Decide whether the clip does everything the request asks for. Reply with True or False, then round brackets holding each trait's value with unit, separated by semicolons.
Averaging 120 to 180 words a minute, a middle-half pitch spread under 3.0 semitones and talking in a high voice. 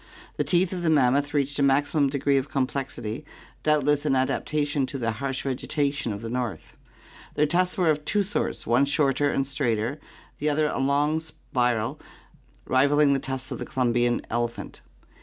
False (175 wpm; 2.5 semitones; 140 Hz)